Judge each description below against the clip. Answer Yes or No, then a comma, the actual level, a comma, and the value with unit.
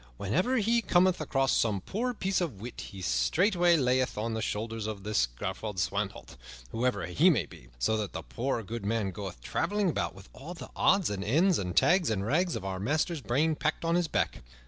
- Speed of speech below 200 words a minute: No, fast, 205 wpm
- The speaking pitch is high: No, low, 125 Hz